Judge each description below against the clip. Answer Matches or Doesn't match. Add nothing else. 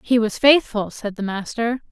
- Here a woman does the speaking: Matches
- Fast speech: Doesn't match